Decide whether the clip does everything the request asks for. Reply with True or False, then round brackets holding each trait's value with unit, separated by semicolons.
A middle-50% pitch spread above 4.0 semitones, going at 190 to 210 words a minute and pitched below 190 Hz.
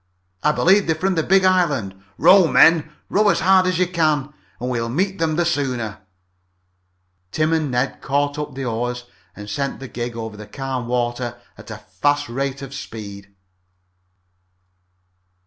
False (5.3 semitones; 165 wpm; 140 Hz)